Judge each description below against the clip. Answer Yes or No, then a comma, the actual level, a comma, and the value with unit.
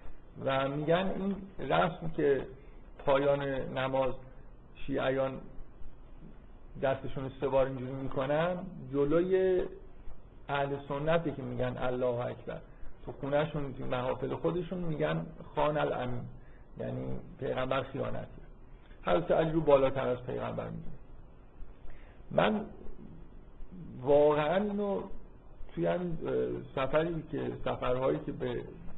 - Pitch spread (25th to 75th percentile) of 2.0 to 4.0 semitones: Yes, average, 3.4 semitones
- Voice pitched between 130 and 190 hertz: Yes, medium, 140 Hz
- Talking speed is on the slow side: Yes, slow, 95 wpm